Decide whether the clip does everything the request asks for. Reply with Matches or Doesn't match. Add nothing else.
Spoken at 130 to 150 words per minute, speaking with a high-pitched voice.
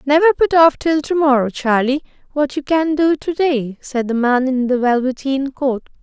Doesn't match